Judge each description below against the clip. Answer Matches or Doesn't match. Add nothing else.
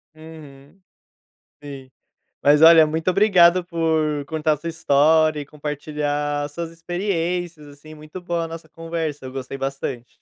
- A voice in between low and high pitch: Matches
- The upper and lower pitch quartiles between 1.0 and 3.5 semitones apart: Matches